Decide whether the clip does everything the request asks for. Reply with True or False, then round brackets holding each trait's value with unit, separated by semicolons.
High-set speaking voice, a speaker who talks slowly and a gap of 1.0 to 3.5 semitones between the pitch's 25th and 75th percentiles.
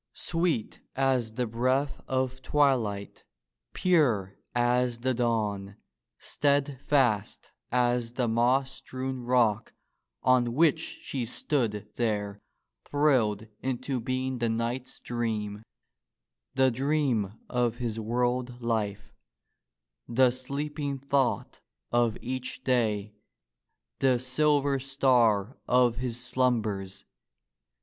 False (125 Hz; 95 wpm; 2.7 semitones)